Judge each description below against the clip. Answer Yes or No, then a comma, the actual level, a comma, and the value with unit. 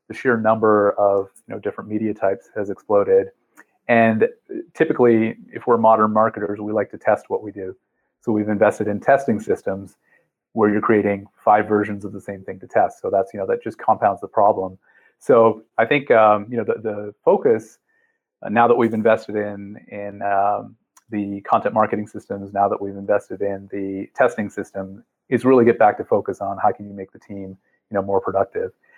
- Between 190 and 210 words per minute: Yes, average, 200 wpm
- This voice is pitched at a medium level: No, low, 105 Hz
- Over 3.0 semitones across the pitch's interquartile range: No, narrow, 2.5 semitones